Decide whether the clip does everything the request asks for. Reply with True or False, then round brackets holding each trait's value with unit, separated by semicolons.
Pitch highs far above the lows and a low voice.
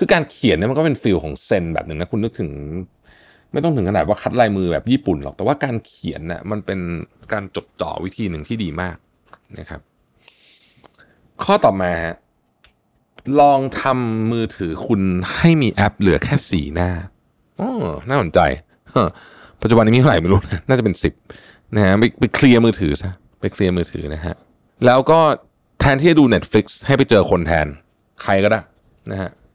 True (5.9 semitones; 100 Hz)